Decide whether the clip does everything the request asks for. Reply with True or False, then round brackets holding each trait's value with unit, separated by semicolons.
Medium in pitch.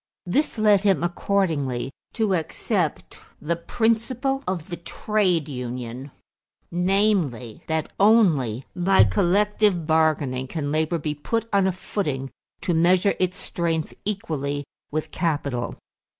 True (170 Hz)